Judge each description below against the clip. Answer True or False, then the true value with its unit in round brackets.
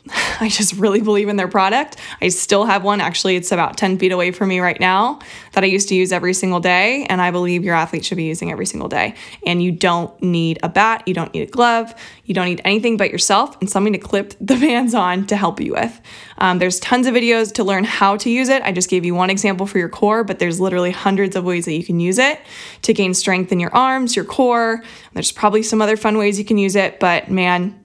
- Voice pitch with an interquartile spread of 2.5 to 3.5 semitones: True (3.0 semitones)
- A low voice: False (195 Hz)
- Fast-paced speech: True (255 wpm)